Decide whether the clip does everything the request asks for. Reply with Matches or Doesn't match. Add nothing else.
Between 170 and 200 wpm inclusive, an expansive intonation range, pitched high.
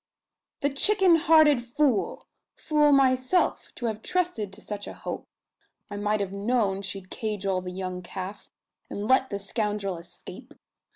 Doesn't match